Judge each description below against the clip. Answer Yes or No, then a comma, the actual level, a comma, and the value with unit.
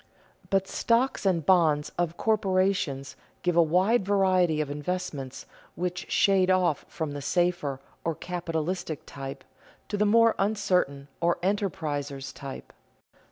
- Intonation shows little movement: No, average, 4.5 semitones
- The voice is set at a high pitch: No, medium, 175 Hz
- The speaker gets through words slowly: Yes, slow, 125 wpm